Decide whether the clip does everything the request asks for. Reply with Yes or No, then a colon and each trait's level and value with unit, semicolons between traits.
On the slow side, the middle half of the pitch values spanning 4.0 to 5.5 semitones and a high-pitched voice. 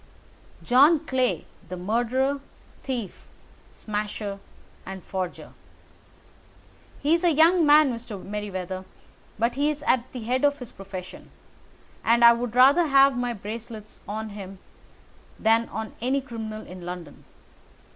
Yes: slow, 125 wpm; average, 4.6 semitones; high, 235 Hz